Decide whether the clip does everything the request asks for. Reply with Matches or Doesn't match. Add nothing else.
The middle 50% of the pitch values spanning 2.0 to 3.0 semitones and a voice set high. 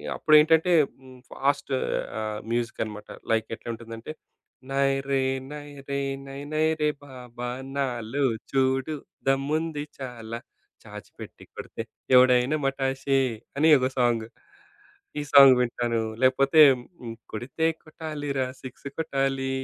Doesn't match